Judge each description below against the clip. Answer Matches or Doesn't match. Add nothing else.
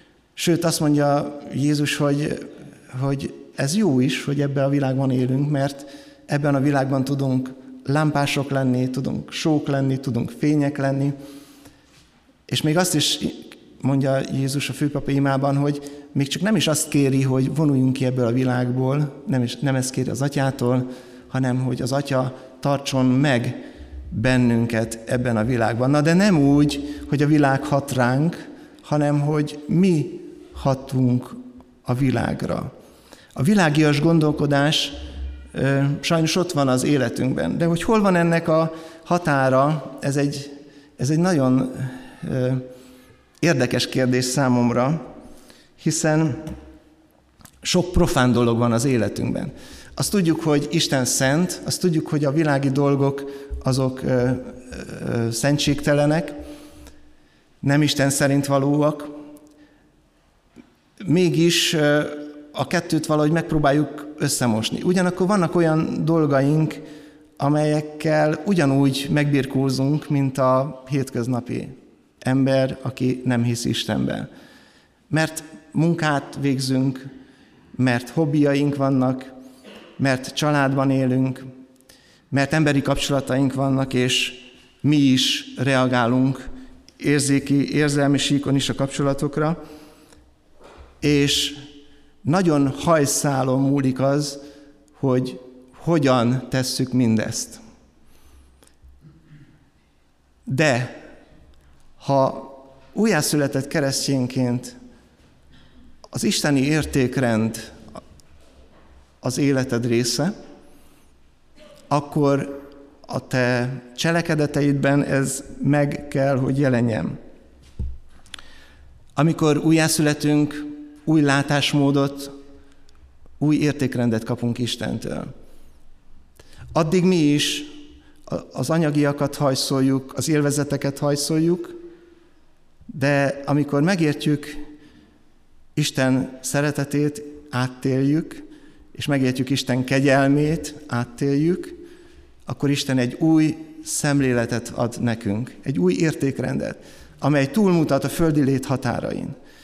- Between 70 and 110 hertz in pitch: Doesn't match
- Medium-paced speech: Doesn't match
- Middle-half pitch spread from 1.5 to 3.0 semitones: Matches